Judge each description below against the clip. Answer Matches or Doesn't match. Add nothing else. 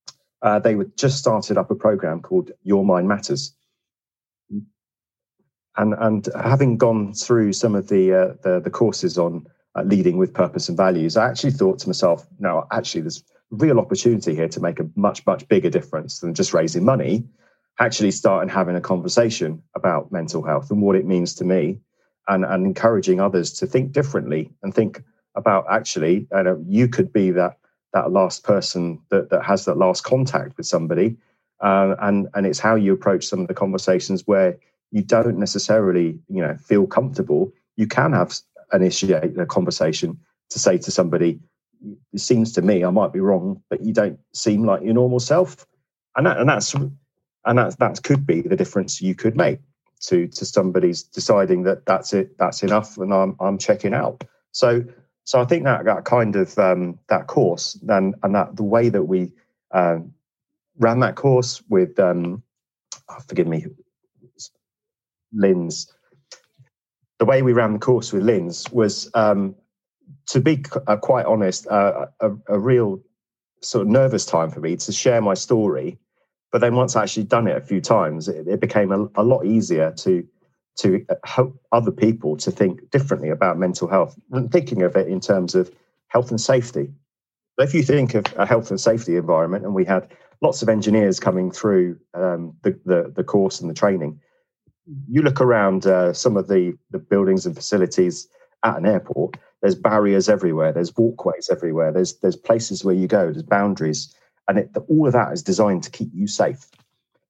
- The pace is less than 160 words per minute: Doesn't match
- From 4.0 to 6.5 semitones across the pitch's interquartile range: Matches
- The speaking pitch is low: Matches